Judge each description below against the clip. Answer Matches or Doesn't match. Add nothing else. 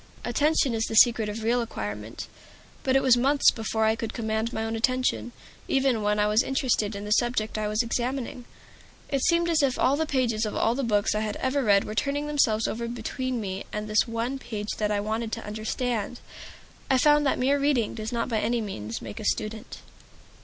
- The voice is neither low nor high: Doesn't match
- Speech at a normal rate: Doesn't match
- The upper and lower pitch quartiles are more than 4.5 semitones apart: Doesn't match